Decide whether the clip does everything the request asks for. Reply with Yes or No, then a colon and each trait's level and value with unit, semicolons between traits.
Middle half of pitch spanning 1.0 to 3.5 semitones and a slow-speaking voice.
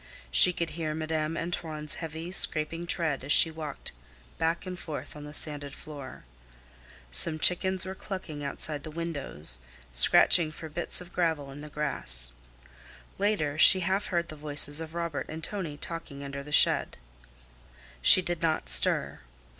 No: narrow, 2.6 semitones; average, 155 wpm